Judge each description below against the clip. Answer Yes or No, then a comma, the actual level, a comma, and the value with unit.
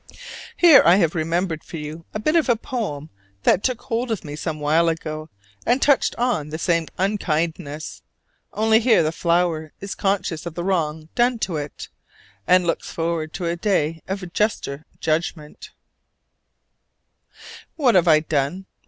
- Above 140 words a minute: Yes, average, 160 wpm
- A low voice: No, medium, 170 Hz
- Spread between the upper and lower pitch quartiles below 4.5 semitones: No, average, 4.8 semitones